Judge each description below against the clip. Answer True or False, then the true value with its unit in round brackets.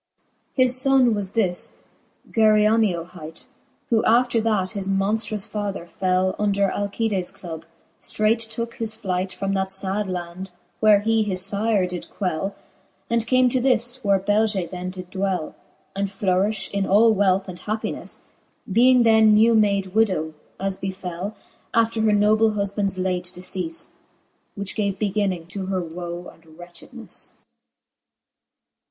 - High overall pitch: True (200 Hz)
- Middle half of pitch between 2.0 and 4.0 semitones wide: True (2.9 semitones)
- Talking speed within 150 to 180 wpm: False (140 wpm)